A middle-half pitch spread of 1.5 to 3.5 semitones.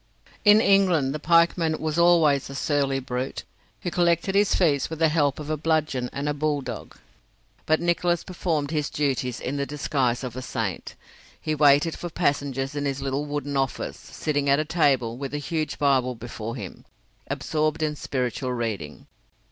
Yes: average, 2.9 semitones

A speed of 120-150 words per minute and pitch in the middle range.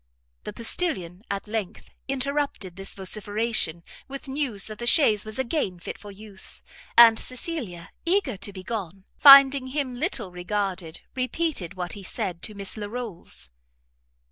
No: average, 140 wpm; high, 215 Hz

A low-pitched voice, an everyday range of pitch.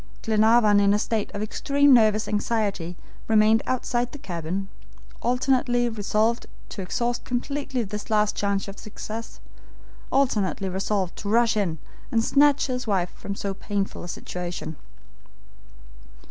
No: high, 215 Hz; average, 3.3 semitones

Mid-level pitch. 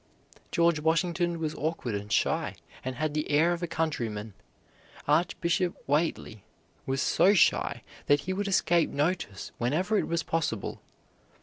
Yes: medium, 160 Hz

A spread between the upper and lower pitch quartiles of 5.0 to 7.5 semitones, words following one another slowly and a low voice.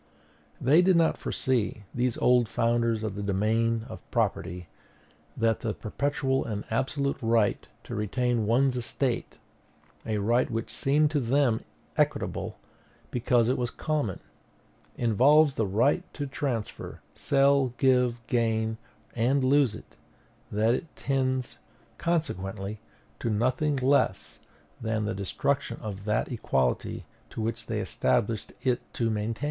No: average, 3.6 semitones; slow, 130 wpm; low, 120 Hz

